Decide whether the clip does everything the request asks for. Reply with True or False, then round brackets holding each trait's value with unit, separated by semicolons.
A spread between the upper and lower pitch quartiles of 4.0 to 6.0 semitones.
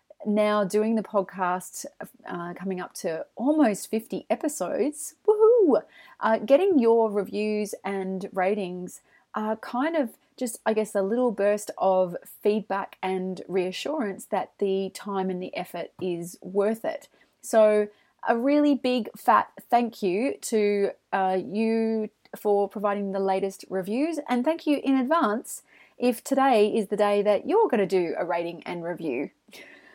True (4.4 semitones)